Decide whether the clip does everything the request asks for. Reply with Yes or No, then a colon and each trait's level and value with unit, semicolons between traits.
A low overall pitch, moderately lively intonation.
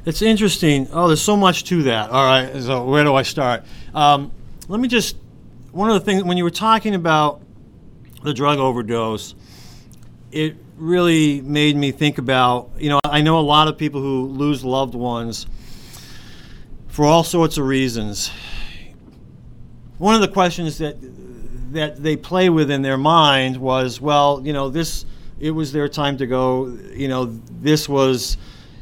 No: medium, 145 Hz; average, 3.5 semitones